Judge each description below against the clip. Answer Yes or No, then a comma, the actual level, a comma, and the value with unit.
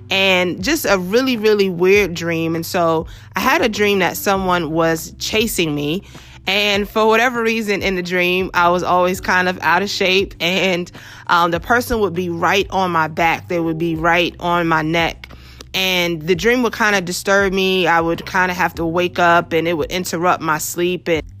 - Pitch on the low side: No, medium, 180 Hz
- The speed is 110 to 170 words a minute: No, fast, 205 wpm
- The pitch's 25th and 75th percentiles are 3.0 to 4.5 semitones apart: No, narrow, 2.6 semitones